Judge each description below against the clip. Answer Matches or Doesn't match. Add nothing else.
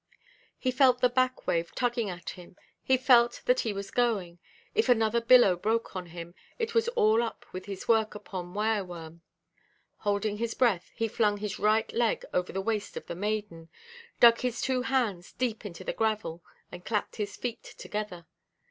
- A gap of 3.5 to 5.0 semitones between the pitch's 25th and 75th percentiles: Matches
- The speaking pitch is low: Doesn't match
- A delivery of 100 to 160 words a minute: Doesn't match